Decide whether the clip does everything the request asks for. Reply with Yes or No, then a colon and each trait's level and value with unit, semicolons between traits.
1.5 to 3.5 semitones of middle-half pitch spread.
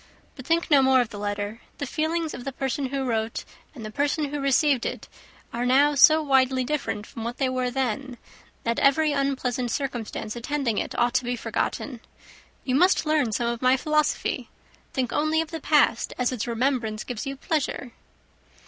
Yes: average, 3.2 semitones